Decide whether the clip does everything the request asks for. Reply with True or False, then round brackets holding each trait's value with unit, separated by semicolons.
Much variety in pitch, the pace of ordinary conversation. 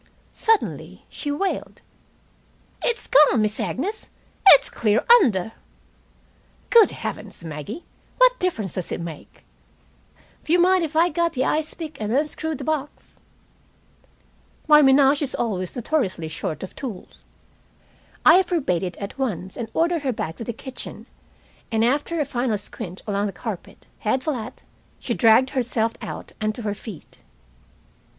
True (6.9 semitones; 145 wpm)